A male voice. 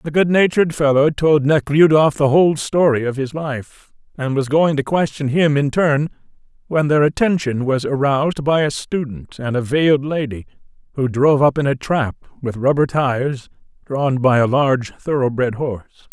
Yes: male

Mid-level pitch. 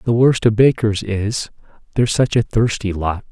No: low, 110 Hz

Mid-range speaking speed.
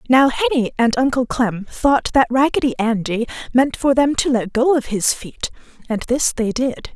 Yes: average, 190 wpm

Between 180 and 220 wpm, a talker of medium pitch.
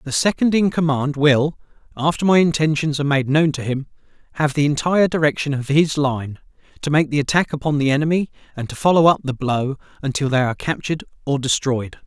Yes: average, 195 wpm; medium, 145 Hz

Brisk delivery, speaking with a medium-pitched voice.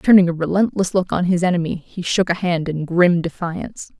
Yes: fast, 210 wpm; medium, 175 Hz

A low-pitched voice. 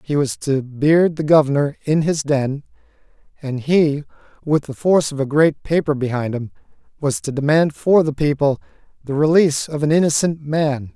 No: medium, 150 Hz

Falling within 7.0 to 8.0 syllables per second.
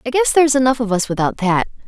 Yes: 7.1 syllables/s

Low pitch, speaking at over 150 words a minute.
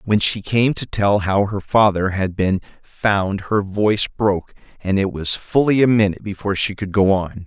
Yes: low, 100 Hz; average, 200 wpm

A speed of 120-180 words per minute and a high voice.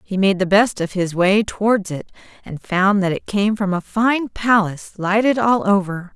No: fast, 205 wpm; high, 200 Hz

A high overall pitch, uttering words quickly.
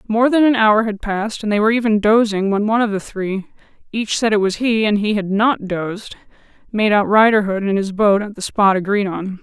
Yes: high, 210 Hz; fast, 225 wpm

